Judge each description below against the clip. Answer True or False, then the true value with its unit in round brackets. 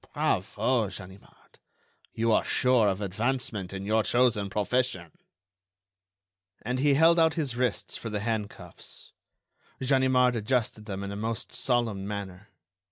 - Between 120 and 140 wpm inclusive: True (135 wpm)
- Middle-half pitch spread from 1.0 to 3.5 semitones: False (4.0 semitones)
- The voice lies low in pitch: True (110 Hz)